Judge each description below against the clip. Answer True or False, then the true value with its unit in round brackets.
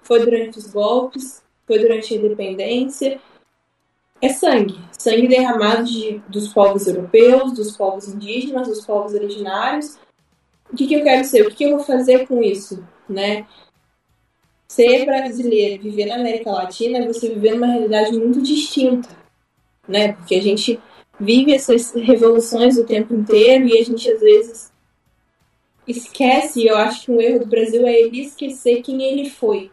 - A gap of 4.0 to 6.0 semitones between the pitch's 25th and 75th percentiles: False (3.3 semitones)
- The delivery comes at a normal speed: True (160 wpm)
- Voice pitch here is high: True (230 Hz)